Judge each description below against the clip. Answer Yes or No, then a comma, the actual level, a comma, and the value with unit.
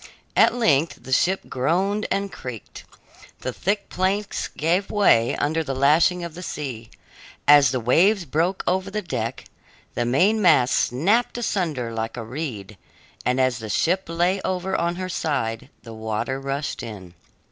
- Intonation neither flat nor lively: No, wide, 7.2 semitones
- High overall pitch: No, medium, 155 Hz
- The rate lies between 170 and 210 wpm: No, average, 155 wpm